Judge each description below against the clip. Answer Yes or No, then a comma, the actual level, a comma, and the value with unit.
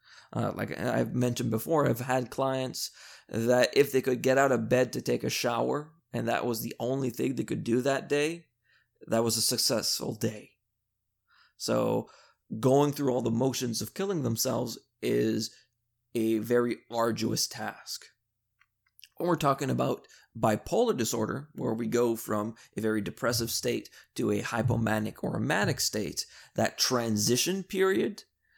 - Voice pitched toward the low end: Yes, low, 120 Hz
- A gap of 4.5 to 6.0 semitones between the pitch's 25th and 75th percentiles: No, narrow, 2.6 semitones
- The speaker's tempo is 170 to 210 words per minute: No, average, 155 wpm